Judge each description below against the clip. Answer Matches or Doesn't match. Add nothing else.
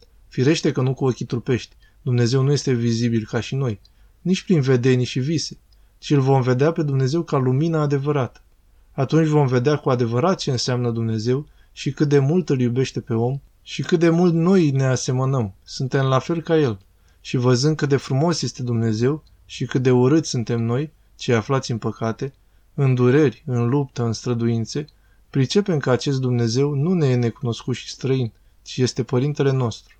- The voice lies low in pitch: Matches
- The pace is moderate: Doesn't match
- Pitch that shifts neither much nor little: Matches